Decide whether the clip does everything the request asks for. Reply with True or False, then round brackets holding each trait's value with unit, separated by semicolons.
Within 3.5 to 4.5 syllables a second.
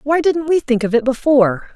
False (5.5 syllables/s)